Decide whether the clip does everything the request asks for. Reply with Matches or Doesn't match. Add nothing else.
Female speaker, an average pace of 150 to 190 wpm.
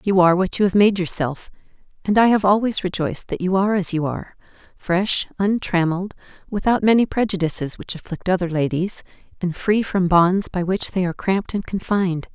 Matches